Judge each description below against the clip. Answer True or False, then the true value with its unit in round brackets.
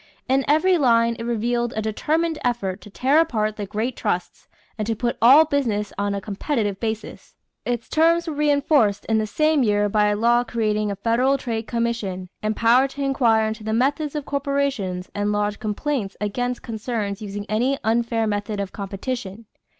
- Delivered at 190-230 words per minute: False (175 wpm)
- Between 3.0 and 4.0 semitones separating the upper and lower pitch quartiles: False (4.4 semitones)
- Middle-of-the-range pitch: False (230 Hz)